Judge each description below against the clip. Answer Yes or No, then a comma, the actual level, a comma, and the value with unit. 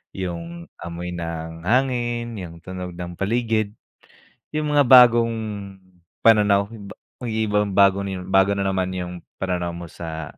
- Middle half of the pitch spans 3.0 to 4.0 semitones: No, average, 4.4 semitones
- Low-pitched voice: Yes, very low, 95 Hz